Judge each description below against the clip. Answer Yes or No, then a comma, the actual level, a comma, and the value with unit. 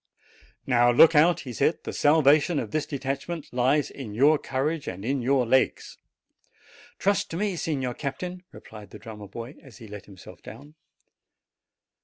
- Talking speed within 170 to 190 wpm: No, average, 160 wpm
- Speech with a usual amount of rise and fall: Yes, average, 4.2 semitones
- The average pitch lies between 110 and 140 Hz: Yes, low, 135 Hz